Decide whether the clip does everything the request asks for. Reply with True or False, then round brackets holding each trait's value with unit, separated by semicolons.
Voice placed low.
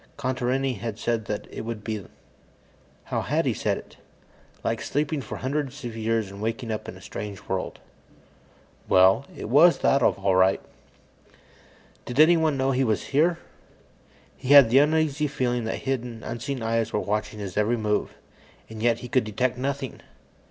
True (120 Hz)